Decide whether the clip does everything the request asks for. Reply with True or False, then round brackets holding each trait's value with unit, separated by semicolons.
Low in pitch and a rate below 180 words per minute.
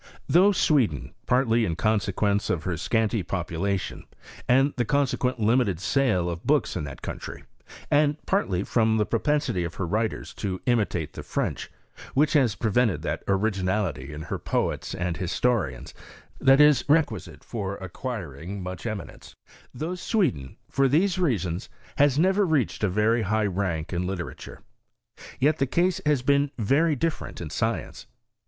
True (110 Hz; 155 wpm)